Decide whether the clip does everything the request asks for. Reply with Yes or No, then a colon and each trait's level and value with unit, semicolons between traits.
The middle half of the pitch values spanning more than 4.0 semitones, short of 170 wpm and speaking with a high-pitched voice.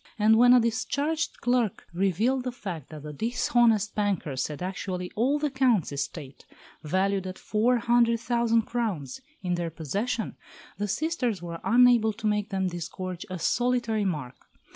Yes: average, 5.1 semitones; average, 155 wpm; high, 215 Hz